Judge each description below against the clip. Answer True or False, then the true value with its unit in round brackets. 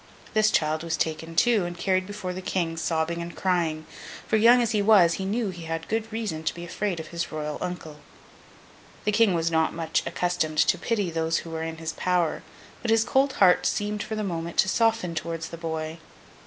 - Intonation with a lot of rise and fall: False (4.2 semitones)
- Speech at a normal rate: False (210 wpm)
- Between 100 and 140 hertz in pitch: False (175 Hz)